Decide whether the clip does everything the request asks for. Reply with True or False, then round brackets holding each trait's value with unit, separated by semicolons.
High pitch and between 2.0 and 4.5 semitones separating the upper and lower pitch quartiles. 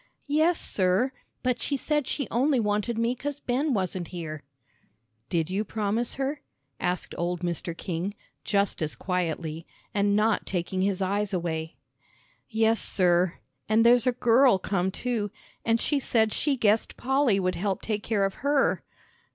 False (210 Hz; 5.2 semitones)